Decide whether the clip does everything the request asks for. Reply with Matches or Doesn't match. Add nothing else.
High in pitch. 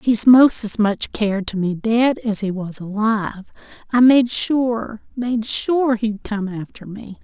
Matches